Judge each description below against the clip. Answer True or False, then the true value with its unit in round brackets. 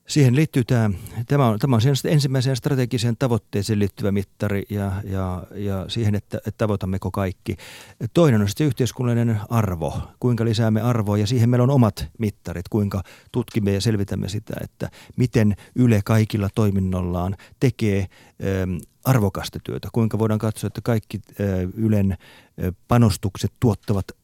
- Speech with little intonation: False (3.3 semitones)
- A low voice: True (110 Hz)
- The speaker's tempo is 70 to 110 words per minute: False (140 wpm)